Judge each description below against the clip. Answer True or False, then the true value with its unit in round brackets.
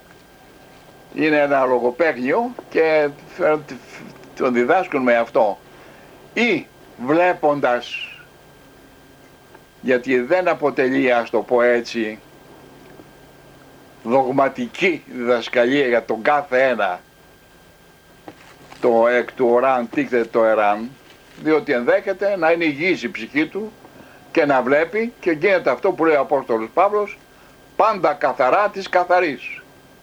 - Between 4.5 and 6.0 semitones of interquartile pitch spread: True (5.6 semitones)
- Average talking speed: False (110 wpm)